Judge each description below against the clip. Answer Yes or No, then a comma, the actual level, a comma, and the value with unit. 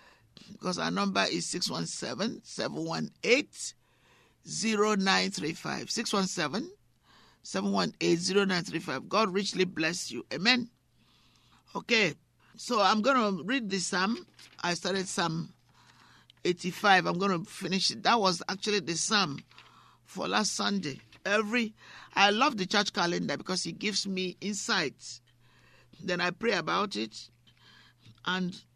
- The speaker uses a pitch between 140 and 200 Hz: Yes, high, 190 Hz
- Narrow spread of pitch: No, average, 3.5 semitones